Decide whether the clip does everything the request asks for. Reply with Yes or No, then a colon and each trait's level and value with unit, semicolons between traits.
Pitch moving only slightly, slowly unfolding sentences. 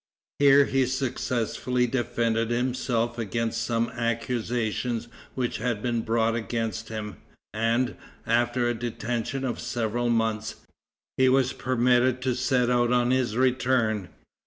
Yes: narrow, 1.7 semitones; slow, 125 wpm